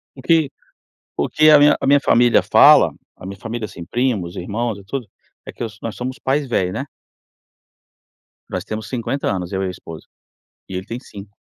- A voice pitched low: Yes, low, 115 Hz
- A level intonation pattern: No, wide, 5.5 semitones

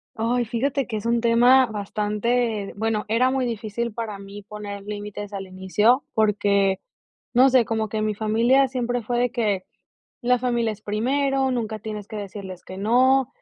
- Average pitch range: Yes, average, 3.0 semitones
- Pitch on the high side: Yes, high, 225 Hz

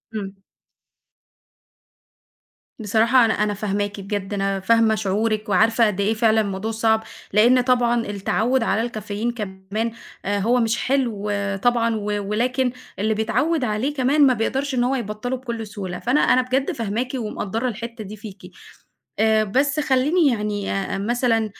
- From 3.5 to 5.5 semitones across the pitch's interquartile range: No, average, 3.0 semitones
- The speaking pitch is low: No, high, 220 Hz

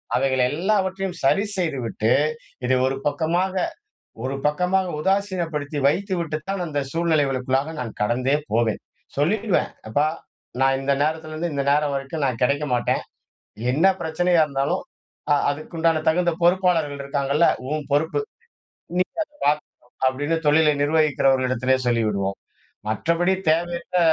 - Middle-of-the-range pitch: Yes, medium, 150 Hz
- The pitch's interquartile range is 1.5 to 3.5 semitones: No, average, 4.2 semitones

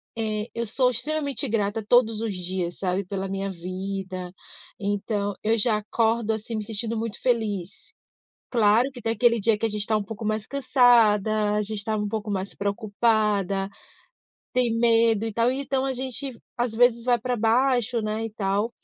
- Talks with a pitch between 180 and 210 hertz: No, high, 220 Hz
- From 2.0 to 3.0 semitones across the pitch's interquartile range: Yes, narrow, 2.5 semitones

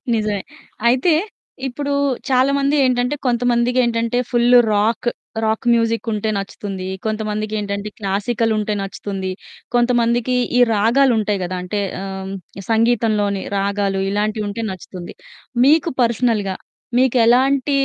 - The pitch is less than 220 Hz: No, high, 225 Hz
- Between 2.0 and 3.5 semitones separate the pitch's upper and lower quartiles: Yes, average, 3.2 semitones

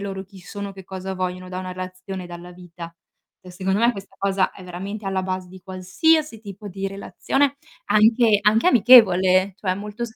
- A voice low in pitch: No, high, 190 Hz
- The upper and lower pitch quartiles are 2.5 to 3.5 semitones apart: No, narrow, 2.1 semitones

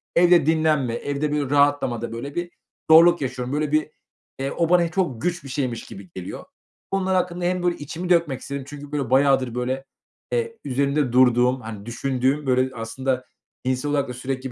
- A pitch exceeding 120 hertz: Yes, medium, 140 Hz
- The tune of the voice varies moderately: Yes, average, 3.9 semitones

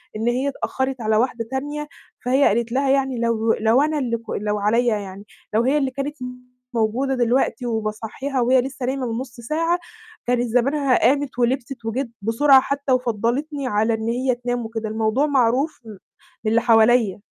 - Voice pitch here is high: Yes, high, 245 Hz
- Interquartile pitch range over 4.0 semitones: No, average, 3.1 semitones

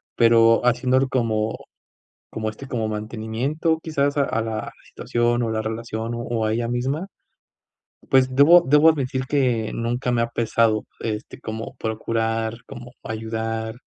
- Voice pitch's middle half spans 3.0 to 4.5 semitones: No, narrow, 2.6 semitones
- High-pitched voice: No, low, 115 Hz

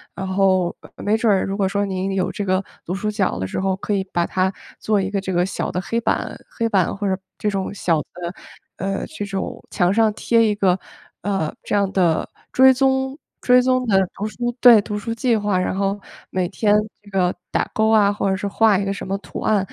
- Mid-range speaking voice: No, high, 200 Hz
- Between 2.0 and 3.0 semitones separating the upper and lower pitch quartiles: Yes, narrow, 2.4 semitones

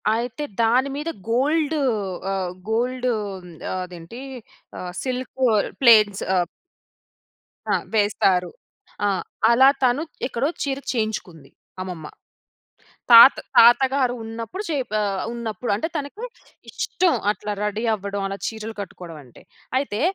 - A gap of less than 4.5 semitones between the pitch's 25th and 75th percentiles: No, average, 4.8 semitones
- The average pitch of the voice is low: No, high, 230 Hz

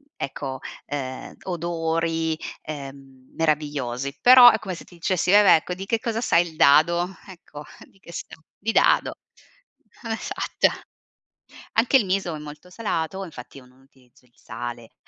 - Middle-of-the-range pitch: Yes, medium, 165 Hz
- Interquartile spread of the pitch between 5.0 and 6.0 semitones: Yes, wide, 5.4 semitones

